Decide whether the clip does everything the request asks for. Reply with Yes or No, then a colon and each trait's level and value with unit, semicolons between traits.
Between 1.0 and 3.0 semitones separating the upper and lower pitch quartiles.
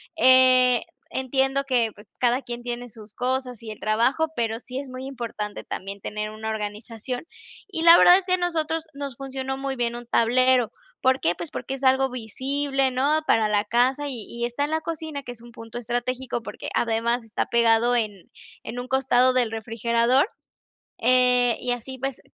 Yes: narrow, 2.5 semitones